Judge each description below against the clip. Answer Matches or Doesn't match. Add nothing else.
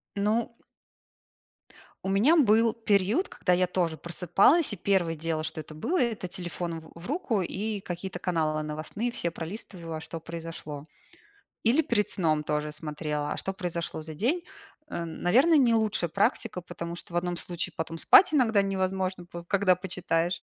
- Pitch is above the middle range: Doesn't match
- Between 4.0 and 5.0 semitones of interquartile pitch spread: Matches